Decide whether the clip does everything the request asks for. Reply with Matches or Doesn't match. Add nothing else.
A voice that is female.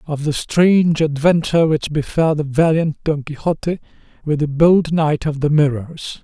Doesn't match